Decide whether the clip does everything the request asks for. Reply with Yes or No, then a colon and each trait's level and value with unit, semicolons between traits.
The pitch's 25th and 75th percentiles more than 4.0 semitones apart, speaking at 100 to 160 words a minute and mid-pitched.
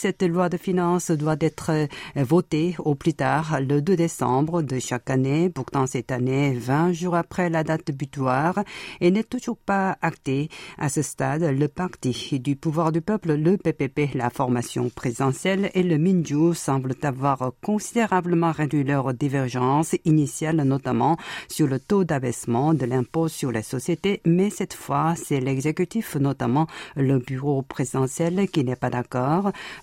Yes: average, 4.5 semitones; average, 155 wpm; medium, 155 Hz